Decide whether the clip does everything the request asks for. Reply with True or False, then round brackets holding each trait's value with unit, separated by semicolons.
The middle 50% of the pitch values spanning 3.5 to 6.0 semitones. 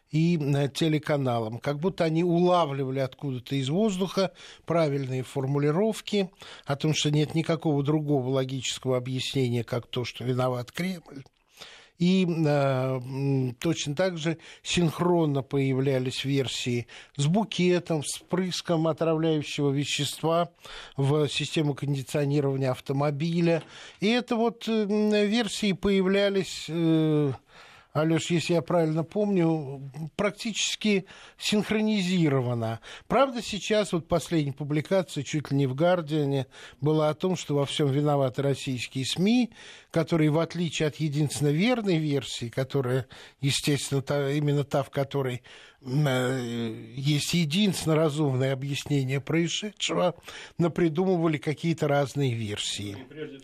True (3.9 semitones)